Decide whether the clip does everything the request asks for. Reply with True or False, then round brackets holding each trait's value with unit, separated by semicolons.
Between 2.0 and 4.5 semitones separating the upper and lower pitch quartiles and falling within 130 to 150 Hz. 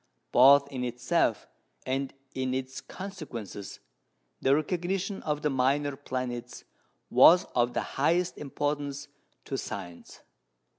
True (2.8 semitones; 140 Hz)